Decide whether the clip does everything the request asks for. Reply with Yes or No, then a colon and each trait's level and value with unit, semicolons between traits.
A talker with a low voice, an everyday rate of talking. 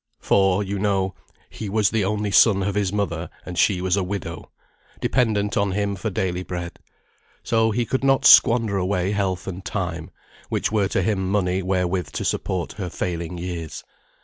Yes: very low, 95 Hz; average, 175 wpm